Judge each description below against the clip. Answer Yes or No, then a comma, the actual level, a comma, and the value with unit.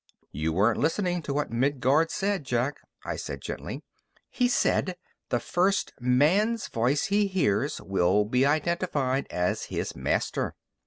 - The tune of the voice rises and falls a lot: Yes, wide, 7.2 semitones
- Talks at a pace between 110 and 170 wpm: Yes, average, 140 wpm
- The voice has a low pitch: No, medium, 145 Hz